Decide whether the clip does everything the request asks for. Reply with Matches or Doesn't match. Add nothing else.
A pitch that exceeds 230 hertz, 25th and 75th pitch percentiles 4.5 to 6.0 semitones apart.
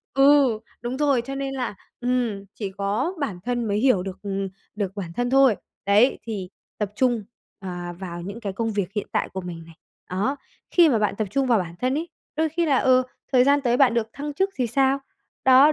Matches